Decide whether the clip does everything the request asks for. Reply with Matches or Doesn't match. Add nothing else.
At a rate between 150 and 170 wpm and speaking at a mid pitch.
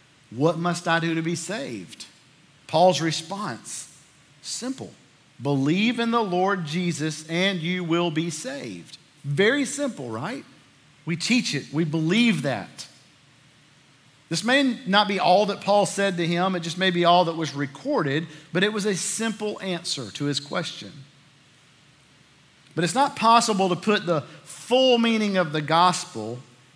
Matches